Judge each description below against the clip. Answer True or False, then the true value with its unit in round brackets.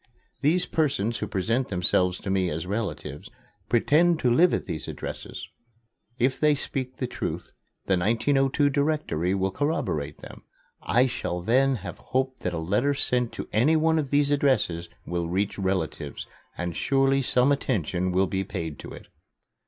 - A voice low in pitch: True (115 Hz)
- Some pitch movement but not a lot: False (7.3 semitones)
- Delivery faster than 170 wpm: False (160 wpm)